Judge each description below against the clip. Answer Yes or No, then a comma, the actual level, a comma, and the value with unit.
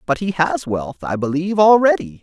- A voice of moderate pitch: Yes, medium, 155 Hz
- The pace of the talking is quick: No, average, 190 wpm